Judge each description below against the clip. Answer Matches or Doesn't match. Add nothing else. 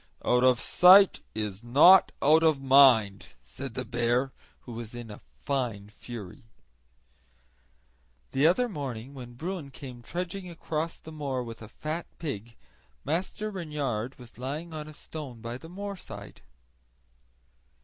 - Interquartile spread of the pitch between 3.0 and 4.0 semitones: Doesn't match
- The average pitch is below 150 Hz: Matches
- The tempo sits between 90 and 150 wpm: Matches